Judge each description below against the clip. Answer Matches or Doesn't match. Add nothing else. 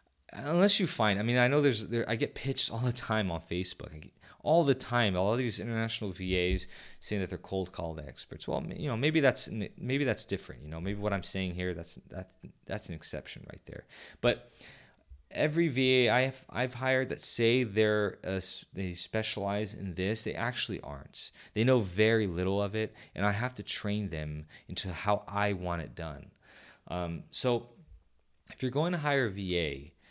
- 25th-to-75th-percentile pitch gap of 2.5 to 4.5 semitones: Doesn't match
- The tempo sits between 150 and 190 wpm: Doesn't match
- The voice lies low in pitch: Matches